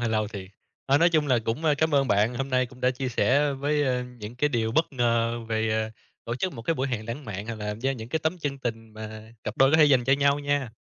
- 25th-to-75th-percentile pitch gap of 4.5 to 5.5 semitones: No, average, 4.1 semitones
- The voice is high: No, low, 125 Hz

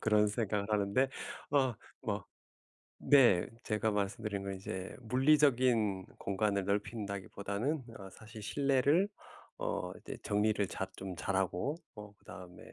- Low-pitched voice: Yes, low, 105 Hz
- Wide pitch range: No, average, 4.1 semitones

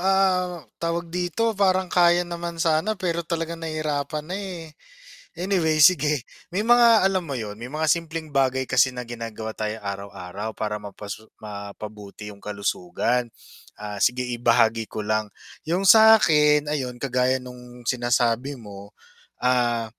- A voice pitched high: No, low, 135 Hz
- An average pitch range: No, wide, 7.4 semitones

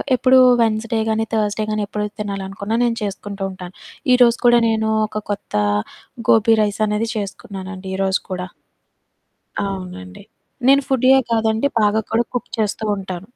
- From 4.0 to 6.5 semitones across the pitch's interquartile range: No, narrow, 2.5 semitones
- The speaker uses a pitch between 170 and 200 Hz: No, high, 210 Hz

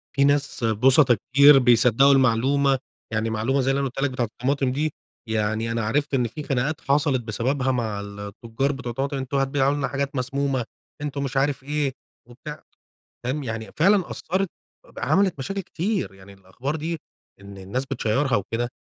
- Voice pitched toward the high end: No, low, 135 Hz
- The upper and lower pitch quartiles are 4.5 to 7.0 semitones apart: No, average, 3.7 semitones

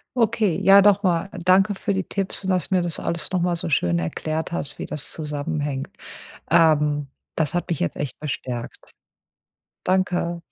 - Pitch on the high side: No, medium, 170 Hz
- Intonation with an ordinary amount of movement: Yes, average, 4.2 semitones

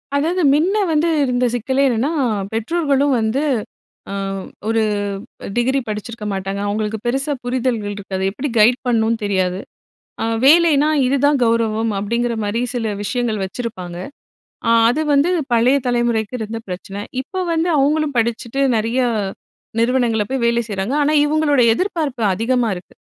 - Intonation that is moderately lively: Yes, average, 4.1 semitones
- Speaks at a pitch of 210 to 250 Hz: Yes, high, 240 Hz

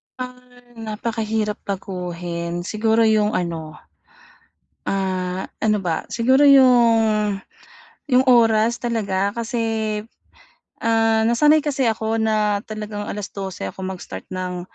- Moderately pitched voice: No, high, 215 Hz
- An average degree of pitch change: Yes, average, 3.3 semitones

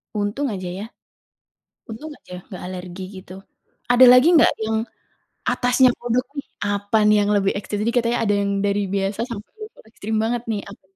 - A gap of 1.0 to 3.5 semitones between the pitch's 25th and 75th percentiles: Yes, average, 3.2 semitones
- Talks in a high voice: Yes, high, 210 Hz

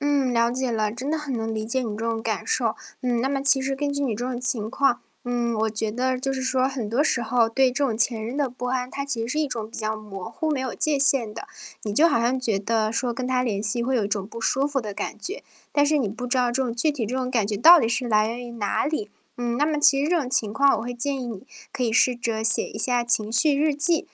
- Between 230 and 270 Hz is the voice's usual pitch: Yes, high, 245 Hz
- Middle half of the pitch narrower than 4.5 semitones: Yes, average, 3.3 semitones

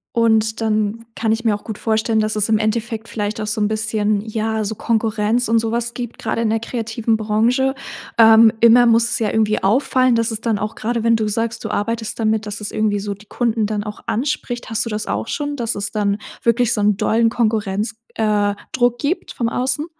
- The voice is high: Yes, high, 220 Hz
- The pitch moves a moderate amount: No, narrow, 1.5 semitones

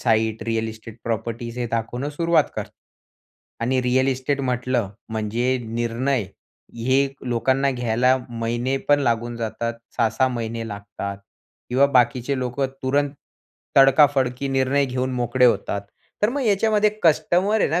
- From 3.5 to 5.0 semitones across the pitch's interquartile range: No, average, 3.0 semitones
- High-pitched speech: No, low, 125 Hz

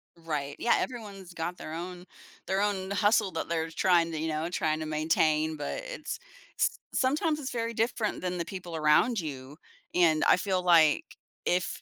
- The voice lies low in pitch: No, medium, 175 Hz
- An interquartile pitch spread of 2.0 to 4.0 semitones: No, average, 4.4 semitones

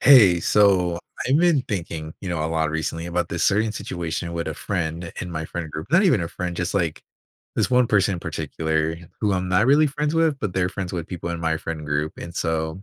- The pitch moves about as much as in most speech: Yes, average, 4.1 semitones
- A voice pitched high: No, very low, 90 Hz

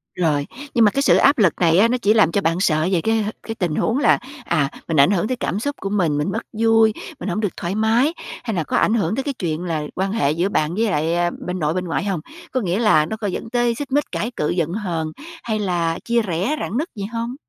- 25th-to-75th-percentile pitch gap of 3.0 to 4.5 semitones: No, average, 5.0 semitones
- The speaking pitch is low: No, high, 200 Hz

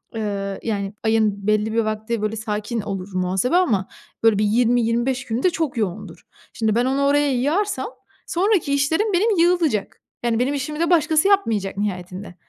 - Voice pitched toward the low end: No, high, 230 Hz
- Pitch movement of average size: No, wide, 6.1 semitones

